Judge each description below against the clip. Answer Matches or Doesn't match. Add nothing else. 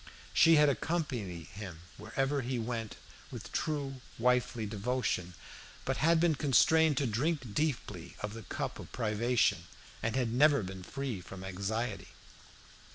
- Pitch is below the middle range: Matches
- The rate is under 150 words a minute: Matches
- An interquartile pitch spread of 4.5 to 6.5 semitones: Matches